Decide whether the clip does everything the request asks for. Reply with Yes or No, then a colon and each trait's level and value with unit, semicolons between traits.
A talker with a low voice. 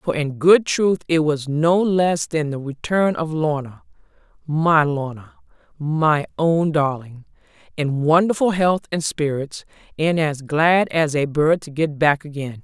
No: medium, 155 Hz